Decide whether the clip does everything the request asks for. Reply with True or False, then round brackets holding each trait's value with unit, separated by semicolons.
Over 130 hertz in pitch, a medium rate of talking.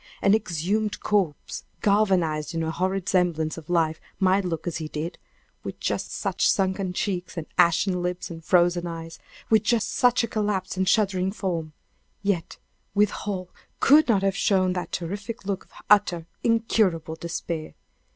True (185 Hz; 155 wpm)